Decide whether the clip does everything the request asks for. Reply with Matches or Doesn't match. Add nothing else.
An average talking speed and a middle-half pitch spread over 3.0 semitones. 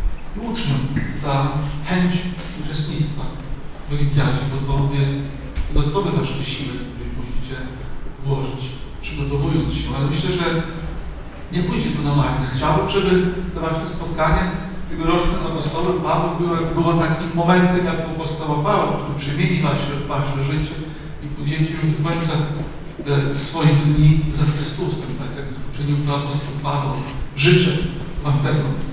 Doesn't match